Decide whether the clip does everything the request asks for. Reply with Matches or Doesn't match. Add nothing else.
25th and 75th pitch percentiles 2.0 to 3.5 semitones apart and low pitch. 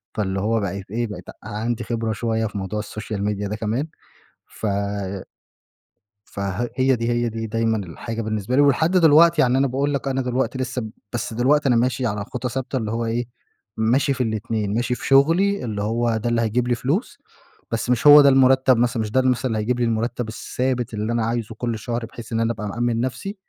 Matches